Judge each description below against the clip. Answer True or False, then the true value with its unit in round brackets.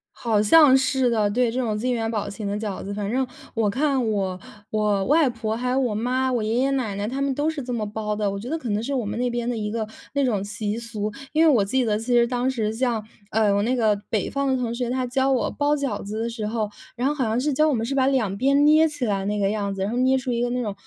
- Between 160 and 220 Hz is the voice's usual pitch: False (235 Hz)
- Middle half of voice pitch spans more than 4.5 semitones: False (3.7 semitones)